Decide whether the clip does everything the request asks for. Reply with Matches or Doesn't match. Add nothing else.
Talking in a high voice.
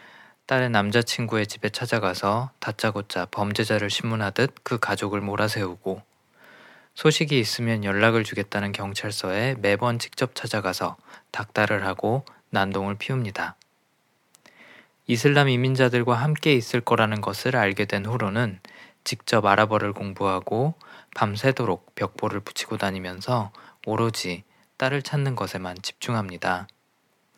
Doesn't match